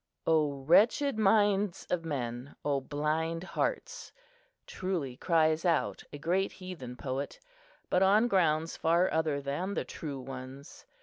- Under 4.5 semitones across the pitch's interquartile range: No, average, 4.8 semitones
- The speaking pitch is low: No, medium, 160 Hz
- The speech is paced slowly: Yes, slow, 130 wpm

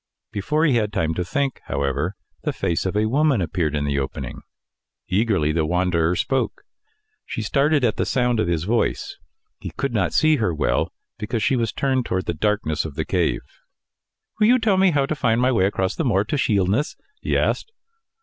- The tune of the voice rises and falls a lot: Yes, wide, 7.6 semitones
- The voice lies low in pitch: Yes, low, 105 Hz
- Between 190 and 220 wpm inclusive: Yes, average, 195 wpm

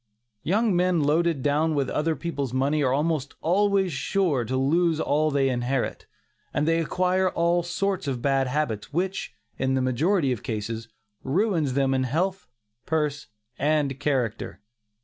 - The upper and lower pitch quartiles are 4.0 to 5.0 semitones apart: Yes, average, 4.3 semitones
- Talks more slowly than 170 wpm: Yes, average, 150 wpm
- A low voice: No, medium, 150 Hz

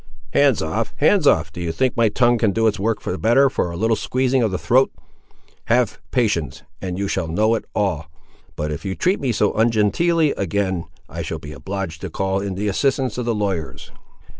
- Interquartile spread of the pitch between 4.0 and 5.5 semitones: Yes, average, 4.9 semitones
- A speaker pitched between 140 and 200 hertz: No, low, 105 Hz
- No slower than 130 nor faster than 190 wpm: No, average, 200 wpm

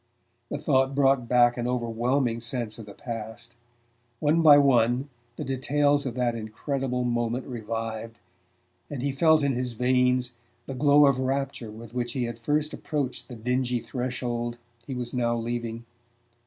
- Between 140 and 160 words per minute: Yes, average, 155 wpm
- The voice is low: Yes, low, 125 Hz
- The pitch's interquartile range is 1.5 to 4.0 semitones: Yes, narrow, 2.4 semitones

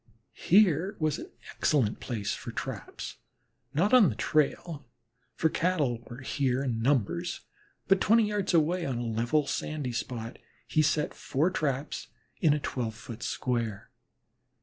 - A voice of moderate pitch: Yes, medium, 145 Hz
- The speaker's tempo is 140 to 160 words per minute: Yes, average, 145 wpm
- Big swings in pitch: Yes, wide, 5.9 semitones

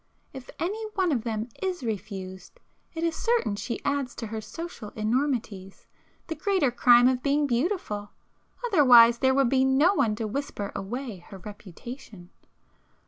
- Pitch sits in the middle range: No, high, 245 Hz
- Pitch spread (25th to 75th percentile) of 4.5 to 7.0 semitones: Yes, average, 5.2 semitones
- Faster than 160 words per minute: No, average, 150 wpm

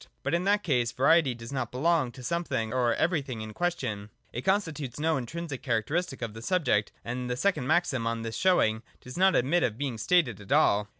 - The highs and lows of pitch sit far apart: Yes, wide, 6.5 semitones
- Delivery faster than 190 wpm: Yes, fast, 205 wpm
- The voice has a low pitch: Yes, low, 130 Hz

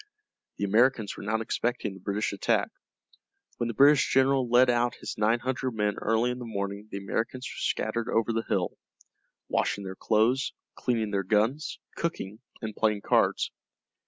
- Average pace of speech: Yes, average, 165 wpm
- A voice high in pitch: No, low, 115 Hz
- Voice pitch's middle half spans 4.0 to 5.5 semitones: No, average, 3.0 semitones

